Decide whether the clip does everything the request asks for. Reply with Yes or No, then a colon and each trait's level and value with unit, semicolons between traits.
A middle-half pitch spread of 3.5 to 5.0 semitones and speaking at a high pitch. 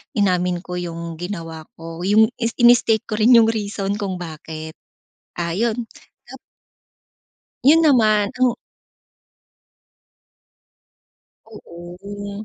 Yes: average, 4.5 semitones; high, 200 Hz